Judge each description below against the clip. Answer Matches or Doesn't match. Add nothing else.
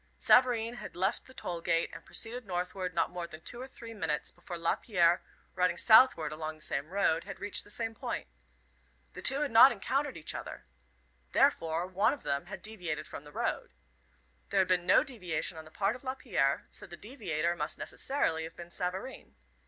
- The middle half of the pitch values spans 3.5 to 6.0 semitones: Matches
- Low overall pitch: Doesn't match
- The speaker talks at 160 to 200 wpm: Matches